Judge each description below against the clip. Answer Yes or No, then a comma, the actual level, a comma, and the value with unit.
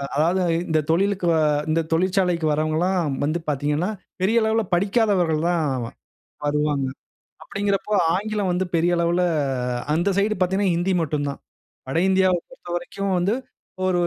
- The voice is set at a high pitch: No, medium, 175 Hz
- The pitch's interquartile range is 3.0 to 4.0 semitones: Yes, average, 3.4 semitones